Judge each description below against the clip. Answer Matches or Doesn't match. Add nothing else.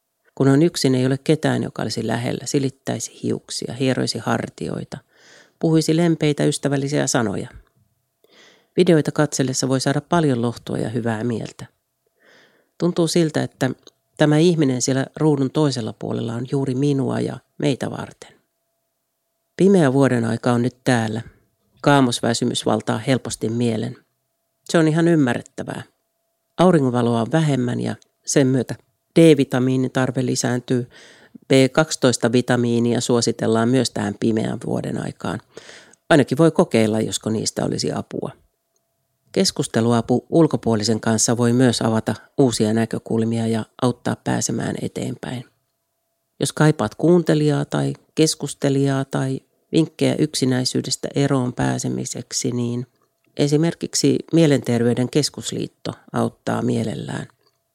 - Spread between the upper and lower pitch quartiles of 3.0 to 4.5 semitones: Matches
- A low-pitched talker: Matches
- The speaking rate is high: Doesn't match